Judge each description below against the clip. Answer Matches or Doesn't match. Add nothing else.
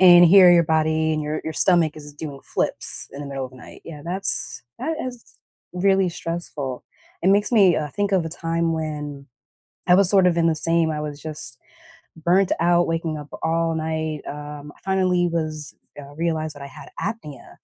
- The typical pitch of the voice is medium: Matches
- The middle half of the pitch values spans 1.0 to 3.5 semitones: Matches